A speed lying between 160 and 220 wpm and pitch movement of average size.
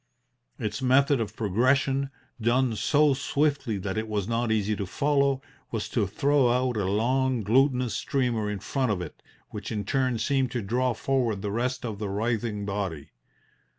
Yes: average, 170 wpm; average, 4.1 semitones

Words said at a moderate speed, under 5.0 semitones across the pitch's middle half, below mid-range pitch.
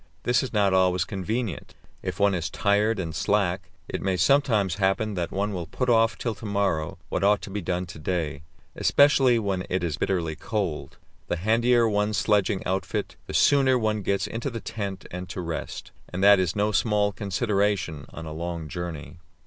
Yes: average, 190 wpm; average, 3.3 semitones; low, 100 Hz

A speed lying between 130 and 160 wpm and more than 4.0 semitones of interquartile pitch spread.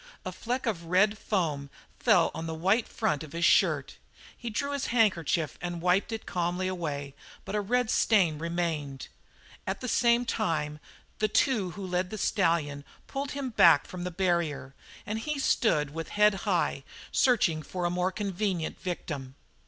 No: average, 170 wpm; average, 4.9 semitones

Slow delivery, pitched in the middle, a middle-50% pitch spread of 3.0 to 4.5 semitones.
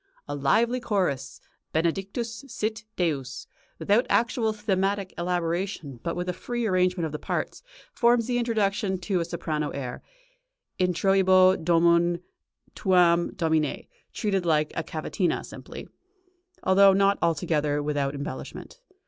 Yes: slow, 125 wpm; medium, 180 Hz; average, 3.8 semitones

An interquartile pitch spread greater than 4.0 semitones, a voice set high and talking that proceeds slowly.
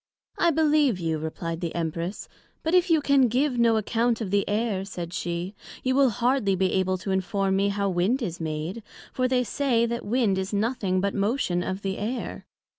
No: average, 5.0 semitones; high, 205 Hz; average, 195 wpm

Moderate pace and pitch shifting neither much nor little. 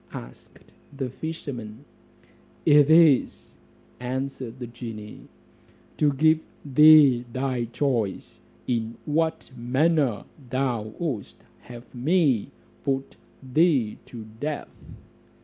No: slow, 95 wpm; average, 4.0 semitones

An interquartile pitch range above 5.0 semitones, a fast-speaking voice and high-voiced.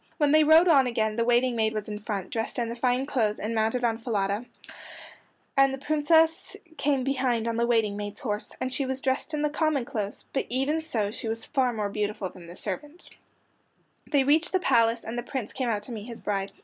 No: average, 4.1 semitones; fast, 225 wpm; high, 240 Hz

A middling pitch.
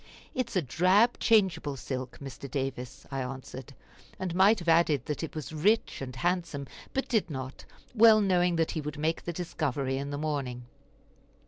Yes: medium, 155 Hz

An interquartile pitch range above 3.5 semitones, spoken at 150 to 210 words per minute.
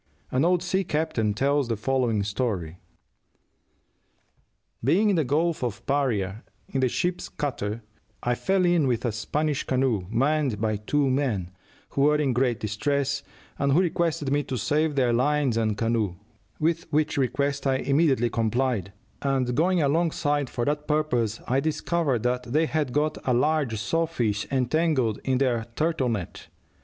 Yes: average, 4.5 semitones; average, 160 wpm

